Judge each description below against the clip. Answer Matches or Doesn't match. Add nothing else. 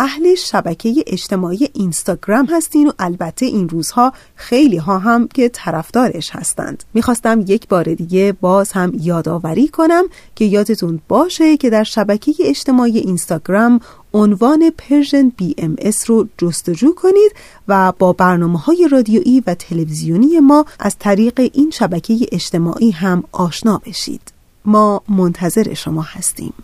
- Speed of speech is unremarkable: Matches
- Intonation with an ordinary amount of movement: Doesn't match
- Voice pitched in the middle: Doesn't match